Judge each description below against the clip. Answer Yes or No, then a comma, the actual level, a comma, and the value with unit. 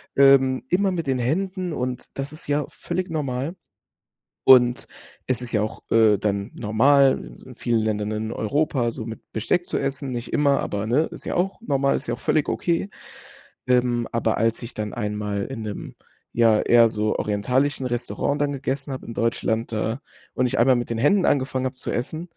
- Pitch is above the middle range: No, low, 125 Hz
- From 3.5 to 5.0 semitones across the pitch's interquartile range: Yes, average, 3.9 semitones